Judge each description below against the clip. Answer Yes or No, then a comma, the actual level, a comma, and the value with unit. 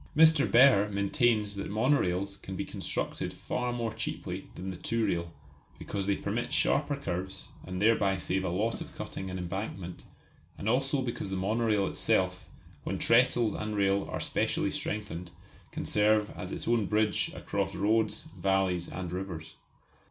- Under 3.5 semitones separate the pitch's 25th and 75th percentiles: Yes, average, 3.1 semitones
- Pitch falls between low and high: No, low, 100 Hz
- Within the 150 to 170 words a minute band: Yes, average, 160 wpm